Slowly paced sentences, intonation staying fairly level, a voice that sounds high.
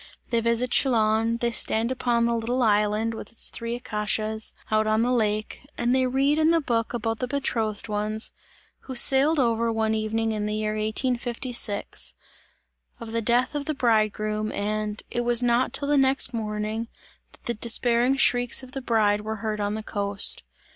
No: average, 180 wpm; narrow, 2.3 semitones; high, 230 Hz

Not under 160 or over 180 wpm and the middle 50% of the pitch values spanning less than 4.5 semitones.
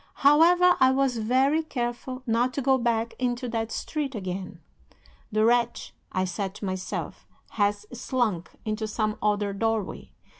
No: average, 145 wpm; average, 3.7 semitones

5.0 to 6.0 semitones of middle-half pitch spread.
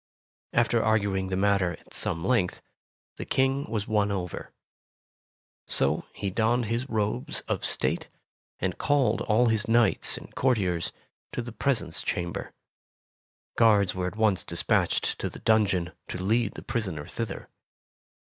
No: average, 3.9 semitones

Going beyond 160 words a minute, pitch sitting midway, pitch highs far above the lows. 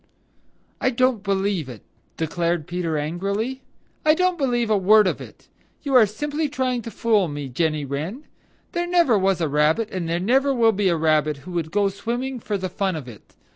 No: average, 195 wpm; high, 200 Hz; wide, 7.0 semitones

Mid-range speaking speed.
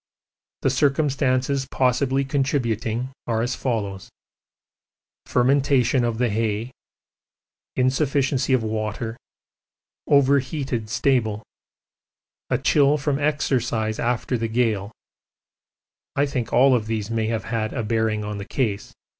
No: slow, 110 wpm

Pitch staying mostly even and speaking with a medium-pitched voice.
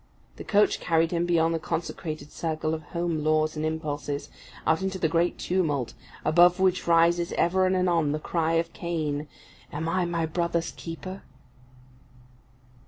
Yes: narrow, 1.9 semitones; medium, 165 Hz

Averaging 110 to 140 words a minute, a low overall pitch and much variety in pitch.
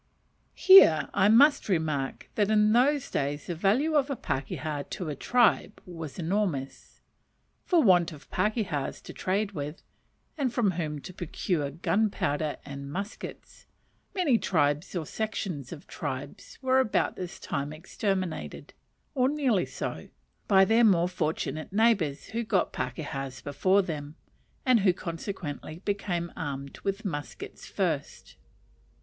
No: slow, 135 wpm; medium, 180 Hz; wide, 6.3 semitones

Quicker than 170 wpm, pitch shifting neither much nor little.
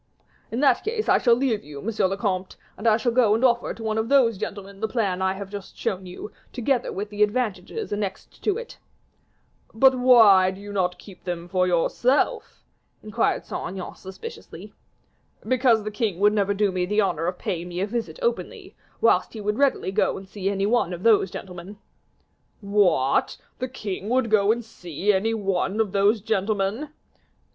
Yes: average, 190 wpm; average, 3.4 semitones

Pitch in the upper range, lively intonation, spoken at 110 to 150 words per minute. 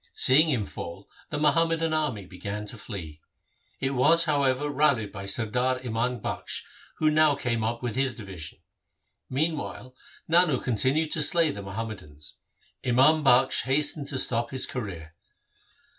No: low, 130 Hz; wide, 5.8 semitones; average, 145 wpm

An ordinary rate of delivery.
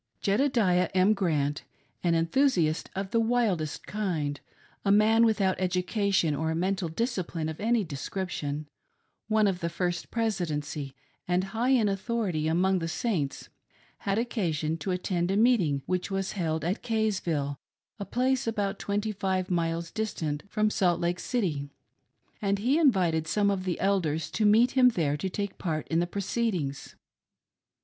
Yes: average, 150 wpm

